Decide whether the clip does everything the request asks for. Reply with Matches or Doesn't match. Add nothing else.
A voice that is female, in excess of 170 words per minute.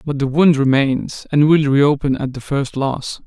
Doesn't match